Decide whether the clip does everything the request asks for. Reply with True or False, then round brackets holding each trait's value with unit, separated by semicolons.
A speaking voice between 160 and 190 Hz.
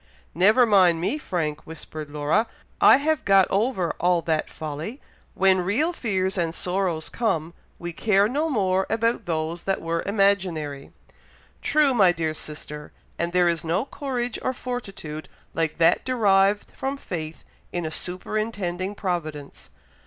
True (185 Hz)